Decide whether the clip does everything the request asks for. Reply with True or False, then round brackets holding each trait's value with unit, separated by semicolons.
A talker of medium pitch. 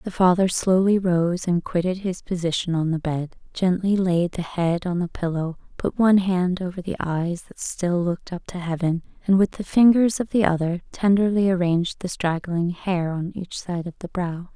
True (180 Hz)